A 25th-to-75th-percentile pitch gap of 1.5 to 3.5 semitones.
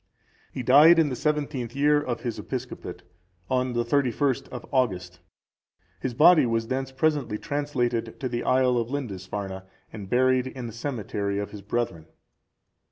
No: average, 4.0 semitones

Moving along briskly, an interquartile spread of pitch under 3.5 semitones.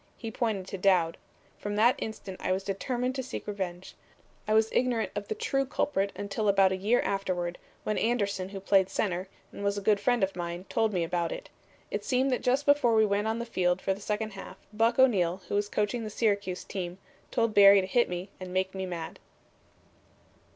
Yes: fast, 210 wpm; average, 3.1 semitones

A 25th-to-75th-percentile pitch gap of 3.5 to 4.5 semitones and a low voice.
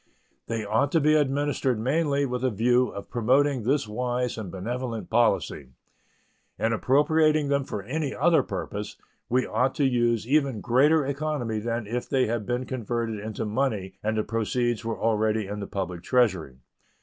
Yes: average, 4.0 semitones; low, 120 Hz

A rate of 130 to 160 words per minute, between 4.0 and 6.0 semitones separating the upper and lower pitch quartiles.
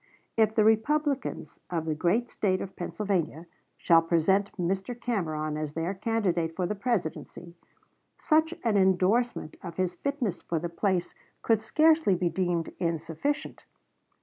Yes: average, 140 wpm; average, 5.0 semitones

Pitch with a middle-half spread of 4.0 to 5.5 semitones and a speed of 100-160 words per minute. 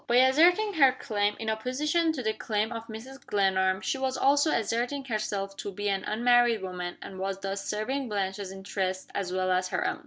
No: average, 5.0 semitones; average, 195 wpm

